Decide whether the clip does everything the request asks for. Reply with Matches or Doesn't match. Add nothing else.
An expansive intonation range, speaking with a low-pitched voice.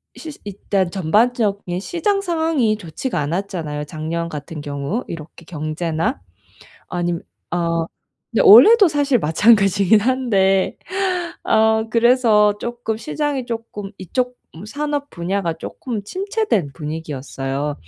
Doesn't match